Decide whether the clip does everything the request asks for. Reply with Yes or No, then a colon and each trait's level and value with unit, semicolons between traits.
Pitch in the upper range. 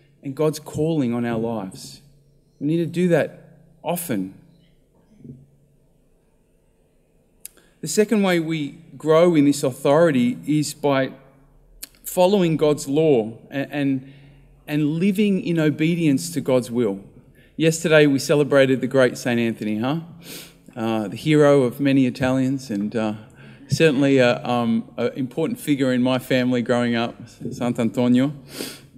No: medium, 140 Hz